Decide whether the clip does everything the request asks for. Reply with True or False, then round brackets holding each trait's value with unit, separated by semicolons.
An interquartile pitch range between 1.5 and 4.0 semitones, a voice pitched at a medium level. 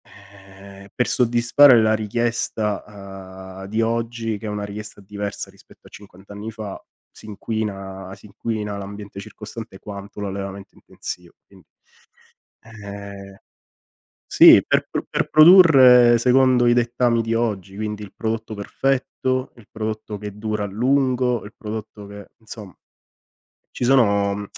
False (2.7 semitones; 105 Hz)